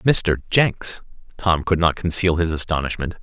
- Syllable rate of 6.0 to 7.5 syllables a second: No, 4.5 syllables/s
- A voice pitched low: Yes, very low, 85 Hz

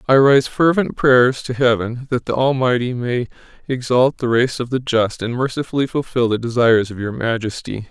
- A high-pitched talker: No, low, 125 Hz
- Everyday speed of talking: Yes, average, 180 wpm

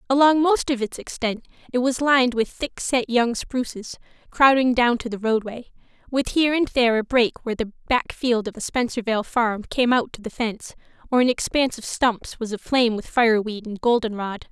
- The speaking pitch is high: Yes, high, 240 Hz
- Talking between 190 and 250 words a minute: Yes, average, 200 wpm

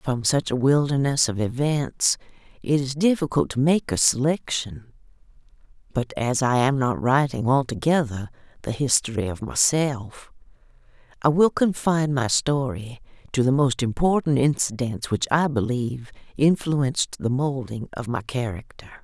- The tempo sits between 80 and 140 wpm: Yes, slow, 135 wpm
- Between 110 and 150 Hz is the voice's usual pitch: Yes, low, 135 Hz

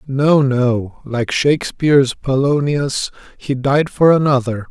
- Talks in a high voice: No, low, 135 Hz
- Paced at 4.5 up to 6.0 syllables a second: No, 3.8 syllables/s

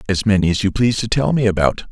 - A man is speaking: Yes, male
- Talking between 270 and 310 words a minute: Yes, fast, 280 wpm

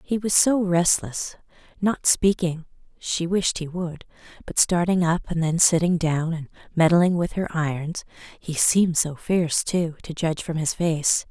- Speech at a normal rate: Yes, average, 170 wpm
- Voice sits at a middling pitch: Yes, medium, 170 Hz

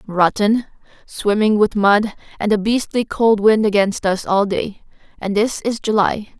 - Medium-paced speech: Yes, average, 160 wpm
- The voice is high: Yes, high, 210 Hz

